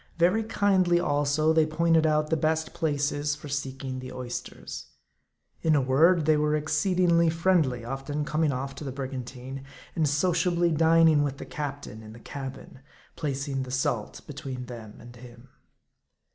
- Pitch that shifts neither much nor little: Yes, average, 3.4 semitones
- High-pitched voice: No, medium, 145 Hz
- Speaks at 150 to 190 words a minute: Yes, average, 160 wpm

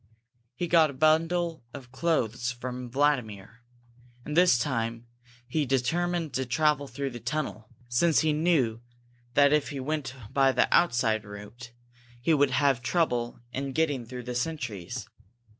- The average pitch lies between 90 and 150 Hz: Yes, low, 135 Hz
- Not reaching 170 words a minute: Yes, average, 145 wpm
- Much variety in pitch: No, average, 4.3 semitones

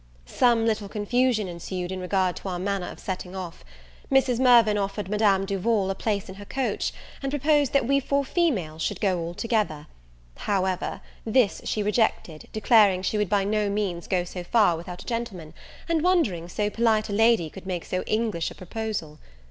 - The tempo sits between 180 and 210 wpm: Yes, average, 185 wpm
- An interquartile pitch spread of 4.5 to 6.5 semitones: No, average, 3.9 semitones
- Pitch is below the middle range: No, high, 205 Hz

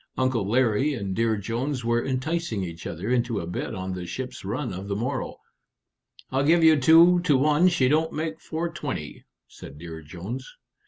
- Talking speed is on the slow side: No, average, 175 wpm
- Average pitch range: No, wide, 7.2 semitones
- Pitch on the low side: Yes, low, 125 Hz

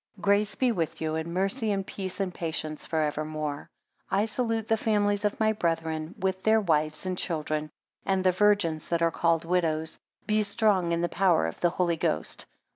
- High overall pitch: No, medium, 180 Hz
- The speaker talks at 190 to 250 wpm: Yes, average, 200 wpm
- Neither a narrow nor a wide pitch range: Yes, average, 4.2 semitones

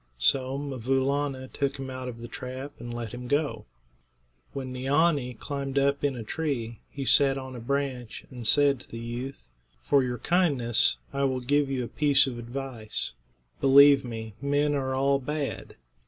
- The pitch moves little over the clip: Yes, narrow, 2.3 semitones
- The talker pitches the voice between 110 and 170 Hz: Yes, low, 135 Hz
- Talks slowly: No, average, 180 wpm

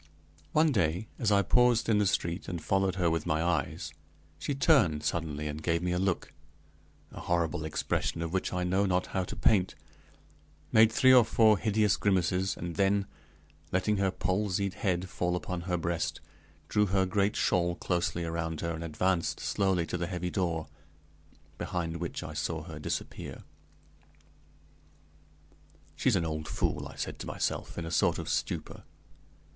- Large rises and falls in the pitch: No, average, 3.0 semitones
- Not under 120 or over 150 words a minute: No, average, 165 wpm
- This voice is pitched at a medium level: No, very low, 90 Hz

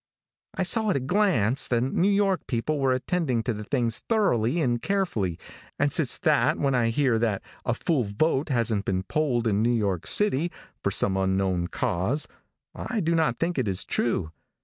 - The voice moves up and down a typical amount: No, wide, 7.3 semitones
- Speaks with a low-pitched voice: Yes, low, 125 Hz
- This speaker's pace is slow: No, average, 185 wpm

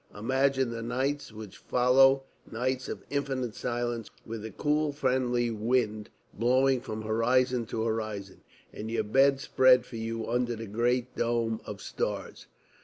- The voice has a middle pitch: No, low, 120 Hz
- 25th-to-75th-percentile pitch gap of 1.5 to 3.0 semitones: Yes, narrow, 2.6 semitones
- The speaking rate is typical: Yes, average, 145 wpm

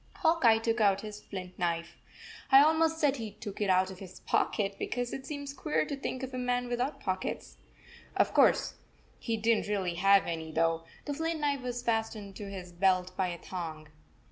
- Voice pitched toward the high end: Yes, high, 210 Hz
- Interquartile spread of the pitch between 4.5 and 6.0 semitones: Yes, wide, 5.5 semitones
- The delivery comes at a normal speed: No, fast, 220 wpm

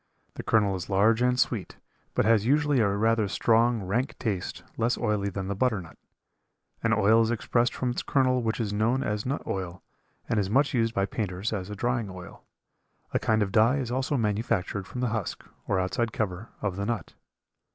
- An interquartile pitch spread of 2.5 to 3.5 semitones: Yes, average, 3.2 semitones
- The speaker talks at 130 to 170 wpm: No, average, 195 wpm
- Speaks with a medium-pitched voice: No, low, 110 Hz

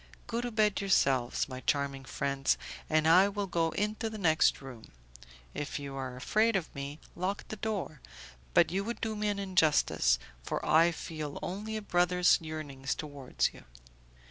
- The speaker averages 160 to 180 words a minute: Yes, average, 170 wpm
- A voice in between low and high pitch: Yes, medium, 165 Hz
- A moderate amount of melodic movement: No, wide, 6.4 semitones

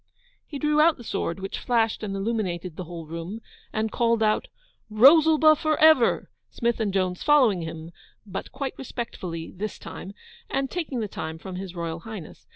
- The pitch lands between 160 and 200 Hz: No, high, 215 Hz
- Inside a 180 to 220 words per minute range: No, average, 170 wpm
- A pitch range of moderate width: No, wide, 6.6 semitones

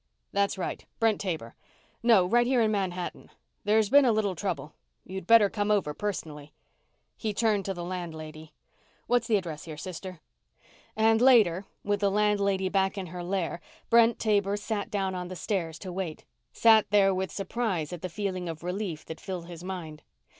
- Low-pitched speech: No, high, 190 Hz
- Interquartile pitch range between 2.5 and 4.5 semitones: Yes, average, 3.2 semitones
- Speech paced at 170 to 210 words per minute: Yes, average, 175 wpm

